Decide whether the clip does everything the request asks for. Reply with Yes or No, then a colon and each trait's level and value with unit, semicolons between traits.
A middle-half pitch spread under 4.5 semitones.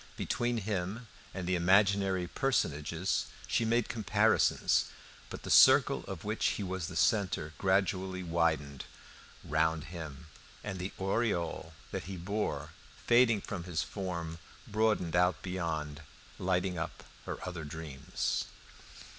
Yes: average, 3.4 semitones